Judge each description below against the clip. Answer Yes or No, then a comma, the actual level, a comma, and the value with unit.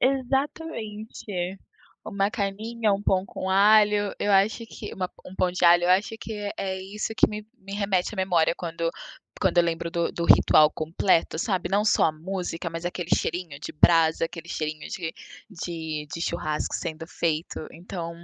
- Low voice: No, medium, 185 Hz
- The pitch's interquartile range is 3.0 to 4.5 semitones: Yes, average, 3.5 semitones